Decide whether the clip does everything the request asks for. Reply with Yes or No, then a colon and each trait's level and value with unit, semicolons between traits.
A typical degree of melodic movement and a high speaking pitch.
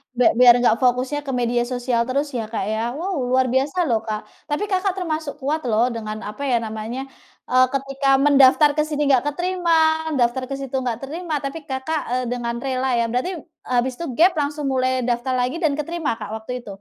Yes: average, 3.7 semitones; very high, 260 Hz